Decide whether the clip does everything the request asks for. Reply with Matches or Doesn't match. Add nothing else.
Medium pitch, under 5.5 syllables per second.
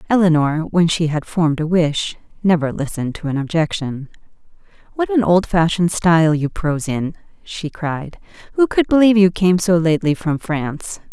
Matches